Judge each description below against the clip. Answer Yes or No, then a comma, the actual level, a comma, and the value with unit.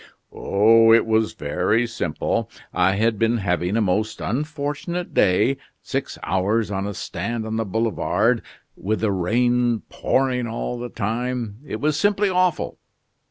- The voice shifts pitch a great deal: No, average, 3.4 semitones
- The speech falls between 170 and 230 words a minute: No, average, 145 wpm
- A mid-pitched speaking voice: No, low, 115 Hz